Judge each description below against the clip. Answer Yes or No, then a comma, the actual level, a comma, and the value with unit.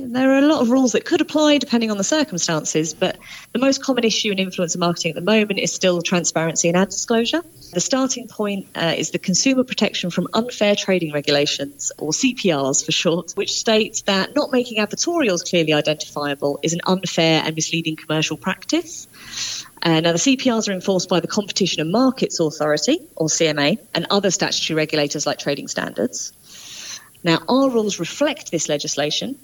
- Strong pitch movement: Yes, wide, 6.4 semitones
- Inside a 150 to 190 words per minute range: Yes, average, 180 wpm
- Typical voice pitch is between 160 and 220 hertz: Yes, medium, 185 Hz